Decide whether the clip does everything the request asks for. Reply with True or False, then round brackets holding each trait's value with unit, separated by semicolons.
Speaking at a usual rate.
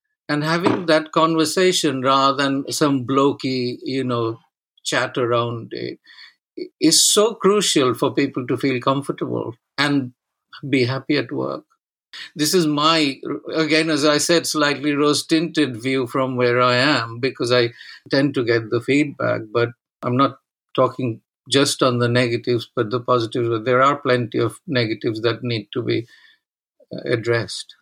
True (145 wpm)